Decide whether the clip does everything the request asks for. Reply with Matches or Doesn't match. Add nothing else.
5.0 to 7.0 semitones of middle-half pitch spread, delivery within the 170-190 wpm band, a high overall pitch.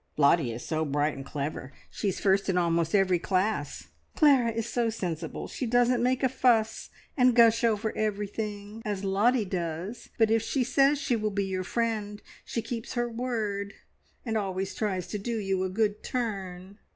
Doesn't match